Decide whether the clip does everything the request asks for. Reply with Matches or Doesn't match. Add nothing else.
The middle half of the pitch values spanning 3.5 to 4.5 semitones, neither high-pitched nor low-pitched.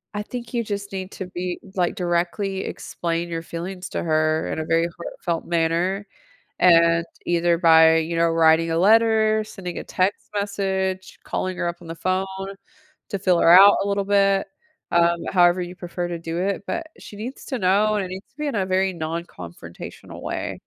Doesn't match